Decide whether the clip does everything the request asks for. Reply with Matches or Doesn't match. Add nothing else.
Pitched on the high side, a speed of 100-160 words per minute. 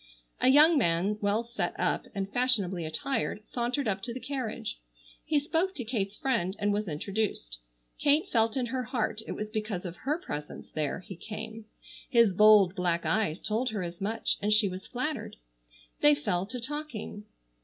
Doesn't match